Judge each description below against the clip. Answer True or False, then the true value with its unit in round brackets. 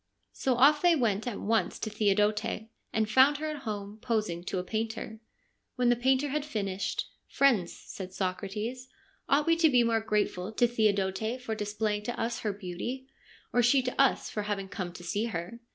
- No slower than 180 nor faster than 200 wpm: True (195 wpm)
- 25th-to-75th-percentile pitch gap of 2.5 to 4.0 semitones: True (3.7 semitones)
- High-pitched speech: True (220 Hz)